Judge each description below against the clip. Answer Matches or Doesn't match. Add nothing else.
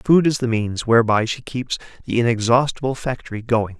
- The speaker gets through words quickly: Doesn't match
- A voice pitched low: Matches